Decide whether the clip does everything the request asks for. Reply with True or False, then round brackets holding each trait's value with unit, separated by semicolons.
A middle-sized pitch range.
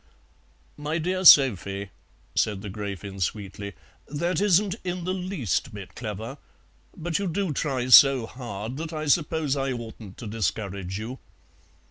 False (7.8 semitones)